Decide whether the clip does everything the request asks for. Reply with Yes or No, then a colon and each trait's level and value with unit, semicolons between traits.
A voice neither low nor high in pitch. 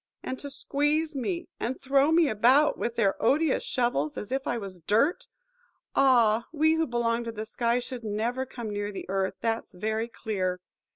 No: high, 235 Hz